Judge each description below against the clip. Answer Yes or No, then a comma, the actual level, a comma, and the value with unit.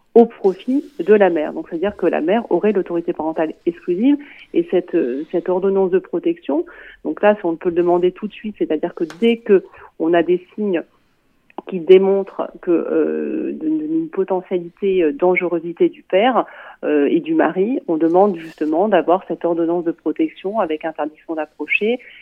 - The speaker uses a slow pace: No, average, 170 wpm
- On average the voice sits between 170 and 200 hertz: Yes, medium, 185 Hz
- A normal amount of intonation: No, wide, 5.8 semitones